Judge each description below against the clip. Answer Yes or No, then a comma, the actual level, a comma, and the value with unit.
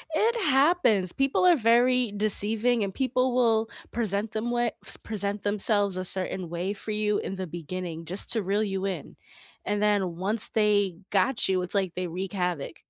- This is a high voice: Yes, high, 205 Hz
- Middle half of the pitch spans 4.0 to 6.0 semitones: No, average, 3.5 semitones